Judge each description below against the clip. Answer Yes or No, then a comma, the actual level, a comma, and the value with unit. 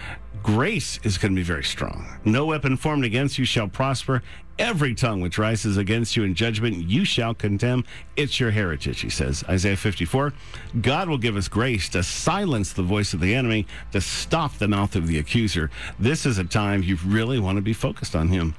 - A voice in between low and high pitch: No, low, 105 Hz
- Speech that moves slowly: No, fast, 205 wpm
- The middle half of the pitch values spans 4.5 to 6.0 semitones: Yes, average, 5.1 semitones